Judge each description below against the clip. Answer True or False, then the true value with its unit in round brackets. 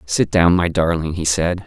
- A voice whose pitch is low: True (85 Hz)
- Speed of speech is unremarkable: False (215 wpm)